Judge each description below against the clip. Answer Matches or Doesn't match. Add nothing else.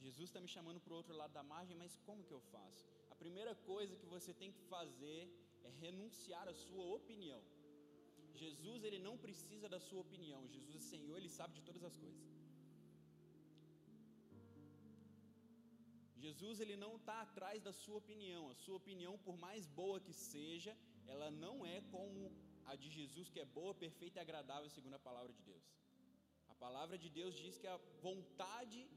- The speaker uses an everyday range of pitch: Doesn't match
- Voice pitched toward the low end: Doesn't match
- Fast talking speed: Matches